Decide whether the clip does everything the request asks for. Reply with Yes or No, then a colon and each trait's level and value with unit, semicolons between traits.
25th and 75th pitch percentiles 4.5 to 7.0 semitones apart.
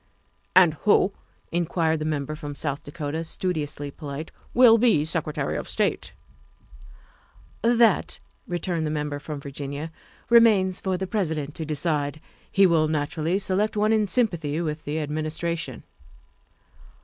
No: average, 4.0 semitones